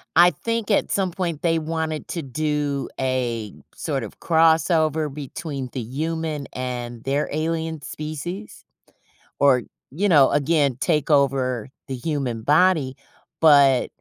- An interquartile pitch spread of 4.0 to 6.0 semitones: No, average, 3.5 semitones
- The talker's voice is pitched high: No, medium, 150 Hz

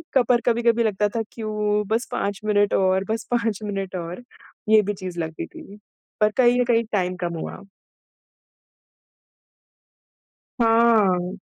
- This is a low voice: No, high, 210 Hz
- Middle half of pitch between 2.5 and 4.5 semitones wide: Yes, average, 3.3 semitones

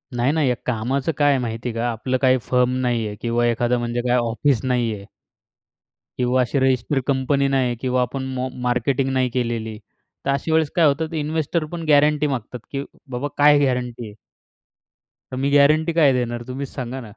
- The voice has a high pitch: No, low, 130 Hz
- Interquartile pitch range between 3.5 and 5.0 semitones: No, average, 2.7 semitones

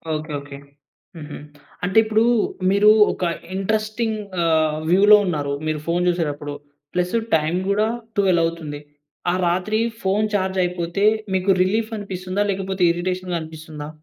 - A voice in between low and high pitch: Yes, medium, 180 Hz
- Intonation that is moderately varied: Yes, average, 3.9 semitones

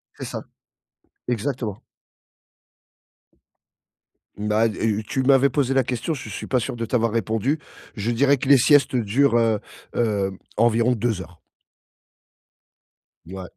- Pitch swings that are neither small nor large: Yes, average, 3.6 semitones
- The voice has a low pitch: Yes, low, 115 Hz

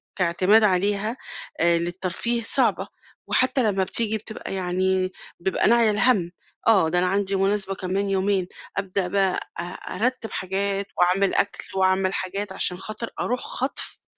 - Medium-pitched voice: No, high, 195 Hz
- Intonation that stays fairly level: Yes, narrow, 2.1 semitones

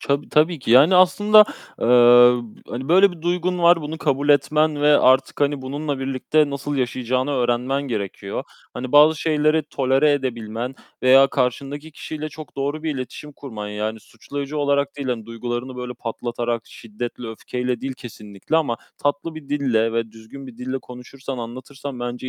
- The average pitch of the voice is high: No, low, 135 Hz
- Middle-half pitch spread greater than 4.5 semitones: No, average, 3.3 semitones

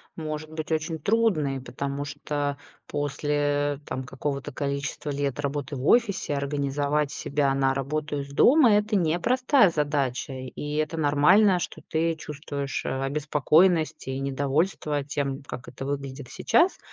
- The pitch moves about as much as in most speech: No, narrow, 2.2 semitones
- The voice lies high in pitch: No, medium, 145 Hz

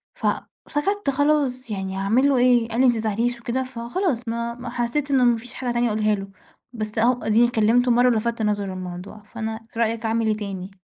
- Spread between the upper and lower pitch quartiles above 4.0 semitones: No, narrow, 2.4 semitones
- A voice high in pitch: Yes, high, 235 Hz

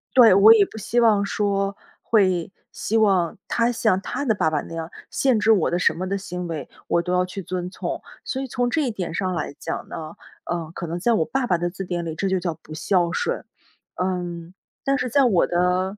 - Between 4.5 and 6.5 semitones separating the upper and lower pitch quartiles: No, average, 4.0 semitones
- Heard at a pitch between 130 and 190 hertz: Yes, medium, 185 Hz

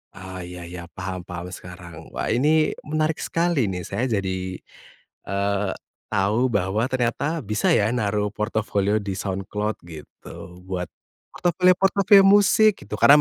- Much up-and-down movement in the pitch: Yes, wide, 8.2 semitones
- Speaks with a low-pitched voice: Yes, low, 105 Hz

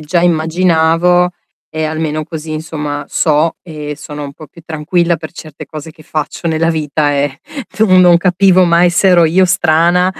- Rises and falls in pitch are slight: Yes, narrow, 2.3 semitones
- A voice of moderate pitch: Yes, medium, 160 Hz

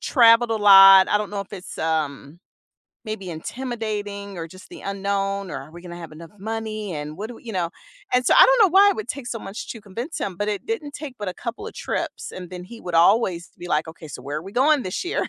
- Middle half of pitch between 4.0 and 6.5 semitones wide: Yes, average, 4.8 semitones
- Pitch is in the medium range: No, high, 200 Hz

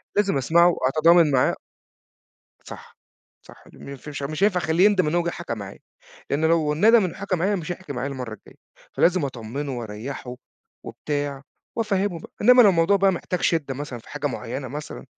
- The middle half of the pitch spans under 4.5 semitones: No, average, 5.1 semitones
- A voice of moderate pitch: Yes, medium, 155 Hz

